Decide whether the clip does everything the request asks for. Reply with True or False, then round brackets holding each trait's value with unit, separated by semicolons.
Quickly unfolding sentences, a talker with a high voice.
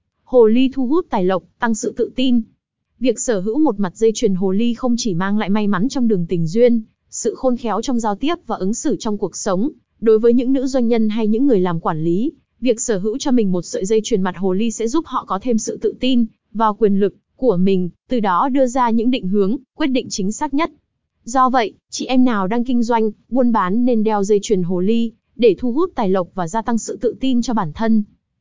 True (255 wpm; 230 Hz)